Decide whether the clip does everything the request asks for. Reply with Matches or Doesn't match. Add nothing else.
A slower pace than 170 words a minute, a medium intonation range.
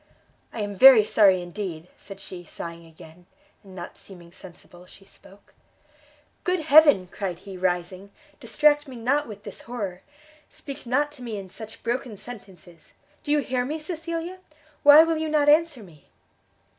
Doesn't match